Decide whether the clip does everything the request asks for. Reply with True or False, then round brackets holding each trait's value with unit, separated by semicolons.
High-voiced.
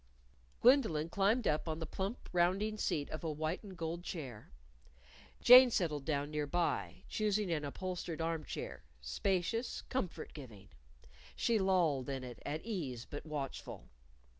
False (165 Hz)